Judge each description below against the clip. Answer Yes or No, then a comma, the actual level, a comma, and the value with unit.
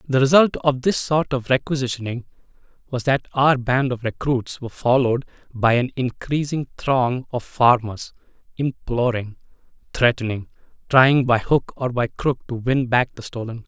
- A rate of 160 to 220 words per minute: No, average, 150 wpm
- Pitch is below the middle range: Yes, low, 125 Hz